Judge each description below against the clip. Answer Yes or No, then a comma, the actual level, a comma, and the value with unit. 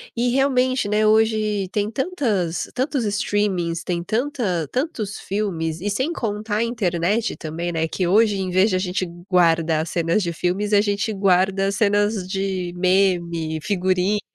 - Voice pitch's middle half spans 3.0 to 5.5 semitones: Yes, average, 3.5 semitones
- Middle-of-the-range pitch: No, high, 200 Hz